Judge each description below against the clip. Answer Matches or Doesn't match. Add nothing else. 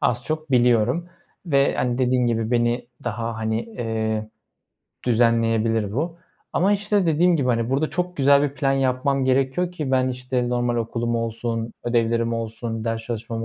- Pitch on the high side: Doesn't match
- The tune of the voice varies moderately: Matches